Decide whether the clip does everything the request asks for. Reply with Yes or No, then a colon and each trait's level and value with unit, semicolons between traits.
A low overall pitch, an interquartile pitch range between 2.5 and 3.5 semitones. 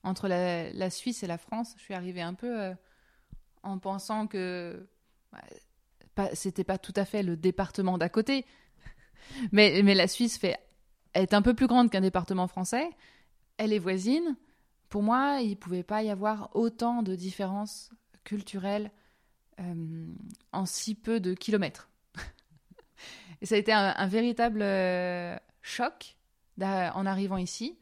No: high, 200 Hz; average, 3.2 semitones